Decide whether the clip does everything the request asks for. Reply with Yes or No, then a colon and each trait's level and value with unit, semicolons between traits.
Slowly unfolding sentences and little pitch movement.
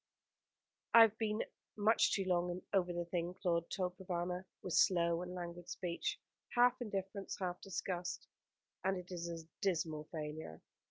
No: average, 150 wpm; narrow, 2.0 semitones